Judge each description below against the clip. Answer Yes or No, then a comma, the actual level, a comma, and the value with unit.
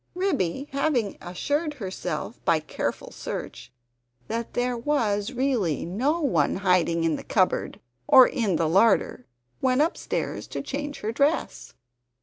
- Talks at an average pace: No, slow, 130 wpm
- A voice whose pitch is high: Yes, high, 230 Hz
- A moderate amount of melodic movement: No, wide, 7.5 semitones